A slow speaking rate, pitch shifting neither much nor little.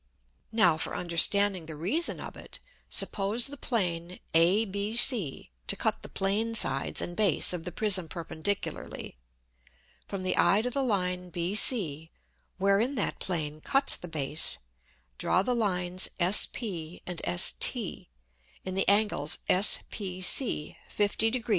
Yes: slow, 130 wpm; average, 4.1 semitones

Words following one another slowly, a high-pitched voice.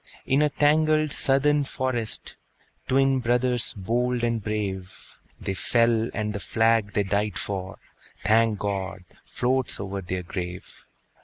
No: slow, 130 wpm; low, 115 Hz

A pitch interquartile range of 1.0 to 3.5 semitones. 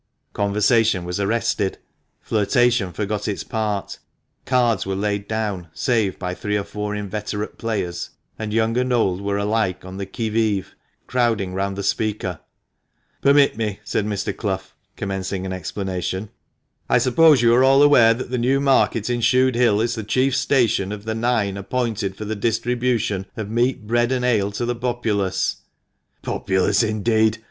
Yes: average, 3.2 semitones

